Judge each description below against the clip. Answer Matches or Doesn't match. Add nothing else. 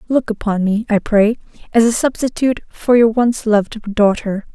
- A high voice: Matches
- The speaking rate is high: Doesn't match